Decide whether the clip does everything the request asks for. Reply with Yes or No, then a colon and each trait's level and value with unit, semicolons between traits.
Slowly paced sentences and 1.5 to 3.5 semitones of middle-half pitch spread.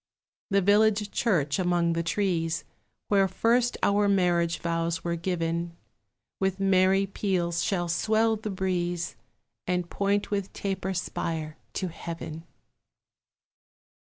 Yes: slow, 115 wpm; average, 2.9 semitones